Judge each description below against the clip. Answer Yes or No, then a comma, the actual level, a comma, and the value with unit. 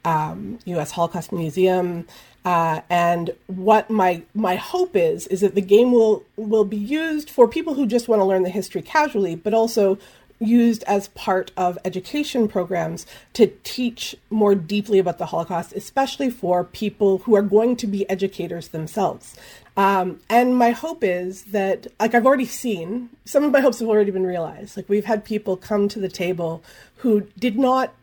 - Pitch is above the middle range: Yes, high, 205 Hz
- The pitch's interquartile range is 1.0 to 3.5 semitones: No, average, 4.3 semitones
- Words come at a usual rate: Yes, average, 180 wpm